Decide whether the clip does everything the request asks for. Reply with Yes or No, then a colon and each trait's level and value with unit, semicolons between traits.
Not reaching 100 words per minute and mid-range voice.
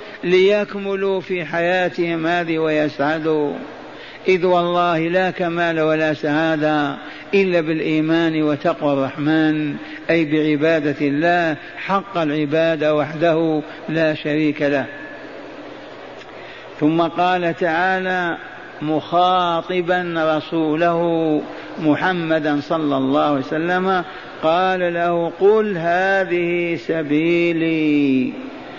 Yes: average, 80 wpm; medium, 165 Hz